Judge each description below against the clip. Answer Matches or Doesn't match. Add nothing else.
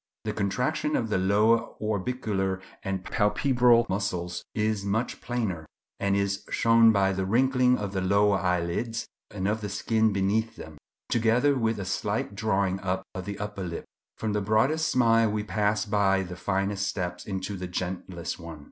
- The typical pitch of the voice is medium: Doesn't match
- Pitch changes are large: Doesn't match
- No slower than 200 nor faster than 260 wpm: Doesn't match